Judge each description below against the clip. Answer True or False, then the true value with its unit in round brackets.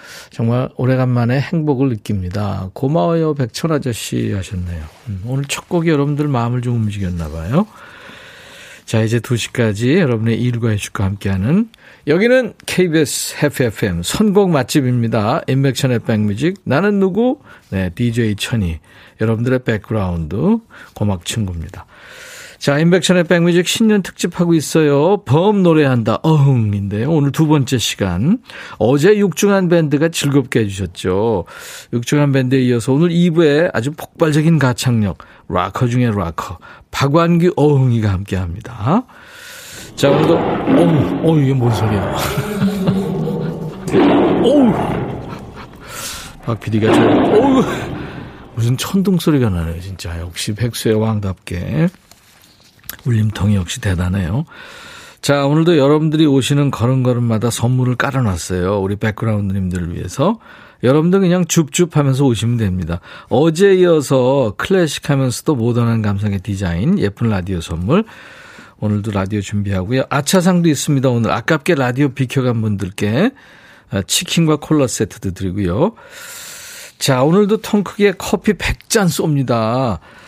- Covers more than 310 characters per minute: False (300 characters per minute)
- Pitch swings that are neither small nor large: False (7.8 semitones)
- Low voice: True (130 Hz)